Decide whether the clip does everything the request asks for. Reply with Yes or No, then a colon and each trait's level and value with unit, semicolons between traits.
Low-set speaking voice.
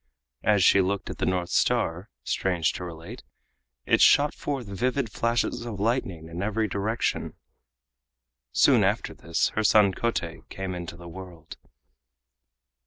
Yes: low, 100 Hz